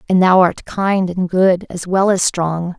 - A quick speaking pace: Yes, fast, 215 wpm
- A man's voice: No, female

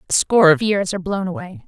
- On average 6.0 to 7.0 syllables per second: Yes, 6.8 syllables/s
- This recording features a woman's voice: Yes, female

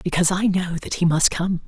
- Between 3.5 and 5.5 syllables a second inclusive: No, 6.5 syllables/s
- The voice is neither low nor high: Yes, medium, 175 Hz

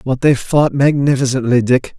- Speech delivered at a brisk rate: No, average, 150 wpm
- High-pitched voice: No, low, 135 Hz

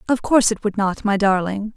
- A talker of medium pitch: No, high, 210 Hz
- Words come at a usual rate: No, fast, 240 wpm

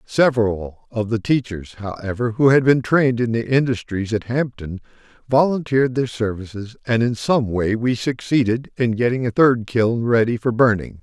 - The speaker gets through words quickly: No, average, 170 wpm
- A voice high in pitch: No, low, 120 Hz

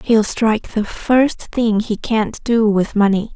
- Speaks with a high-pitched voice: Yes, high, 220 Hz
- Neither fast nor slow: Yes, average, 180 wpm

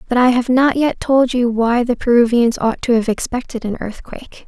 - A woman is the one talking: Yes, female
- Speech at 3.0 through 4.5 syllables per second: No, 5.2 syllables/s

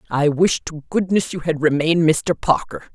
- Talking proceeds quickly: No, average, 185 wpm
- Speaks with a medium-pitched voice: Yes, medium, 160 Hz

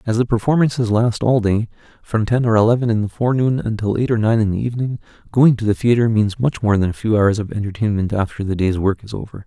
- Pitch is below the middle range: Yes, low, 110 Hz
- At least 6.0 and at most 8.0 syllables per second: Yes, 6.3 syllables/s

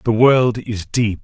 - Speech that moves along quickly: No, average, 195 wpm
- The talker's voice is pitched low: Yes, low, 110 Hz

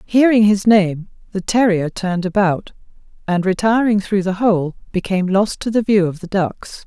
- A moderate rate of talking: Yes, average, 175 wpm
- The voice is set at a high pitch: Yes, high, 195 Hz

